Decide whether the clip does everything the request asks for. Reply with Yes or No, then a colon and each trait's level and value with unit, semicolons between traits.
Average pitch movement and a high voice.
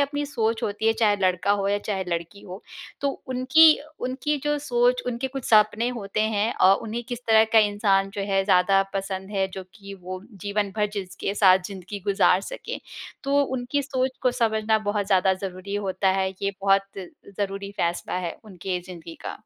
Yes: average, 3.7 semitones; high, 205 Hz